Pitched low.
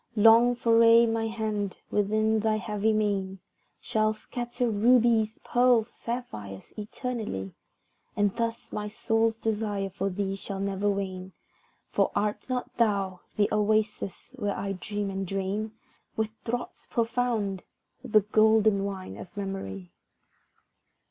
No: high, 215 Hz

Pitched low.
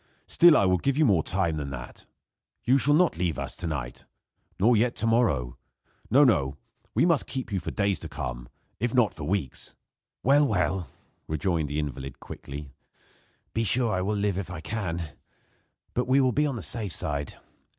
Yes: very low, 95 Hz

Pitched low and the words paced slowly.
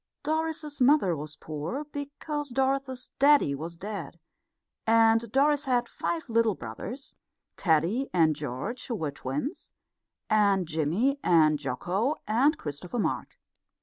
No: high, 225 Hz; slow, 125 wpm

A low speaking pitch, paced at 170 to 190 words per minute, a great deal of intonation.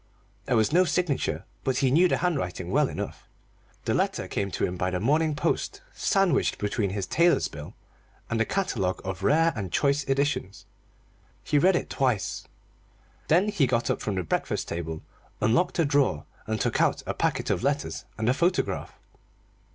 Yes: low, 130 Hz; average, 175 wpm; wide, 8.6 semitones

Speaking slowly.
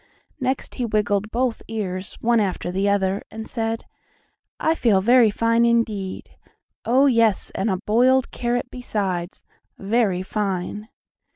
Yes: slow, 130 wpm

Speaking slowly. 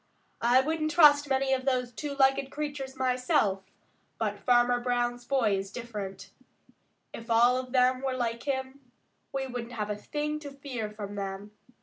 No: average, 160 wpm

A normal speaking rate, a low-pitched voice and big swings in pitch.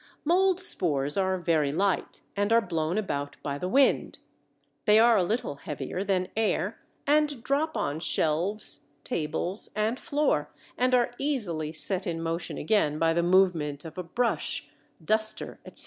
No: average, 155 wpm; high, 190 Hz; wide, 6.2 semitones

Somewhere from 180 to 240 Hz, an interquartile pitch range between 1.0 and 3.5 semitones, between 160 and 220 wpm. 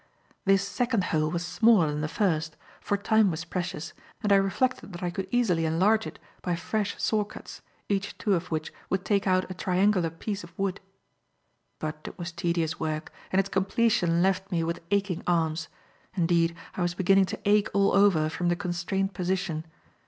Yes: medium, 185 Hz; average, 2.9 semitones; average, 185 wpm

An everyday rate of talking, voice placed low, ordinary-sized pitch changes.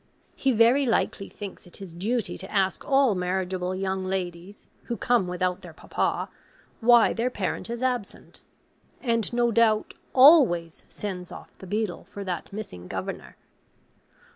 No: average, 145 wpm; high, 200 Hz; average, 4.3 semitones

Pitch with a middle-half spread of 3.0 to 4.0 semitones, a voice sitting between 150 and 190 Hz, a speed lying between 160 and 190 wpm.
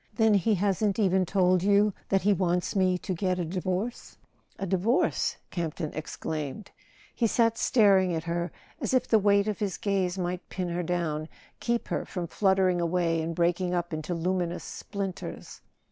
No: narrow, 2.6 semitones; medium, 185 Hz; average, 175 wpm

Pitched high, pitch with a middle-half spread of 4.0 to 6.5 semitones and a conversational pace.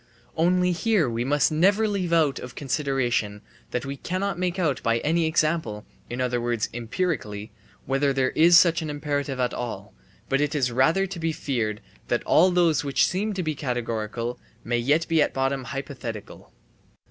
No: medium, 140 Hz; wide, 5.5 semitones; average, 175 wpm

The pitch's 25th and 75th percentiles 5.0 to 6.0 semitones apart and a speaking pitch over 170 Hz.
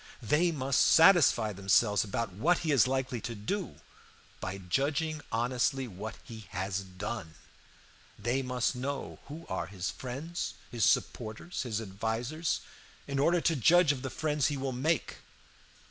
No: wide, 5.6 semitones; low, 125 Hz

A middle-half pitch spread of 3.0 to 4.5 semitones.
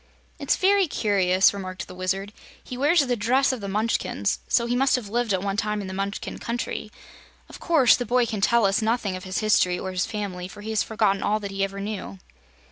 Yes: average, 3.5 semitones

